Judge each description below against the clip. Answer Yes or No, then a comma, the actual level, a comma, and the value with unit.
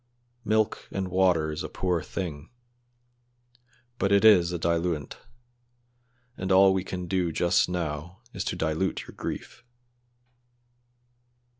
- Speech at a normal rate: No, slow, 125 wpm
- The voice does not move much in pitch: Yes, narrow, 2.3 semitones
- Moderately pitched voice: No, very low, 90 Hz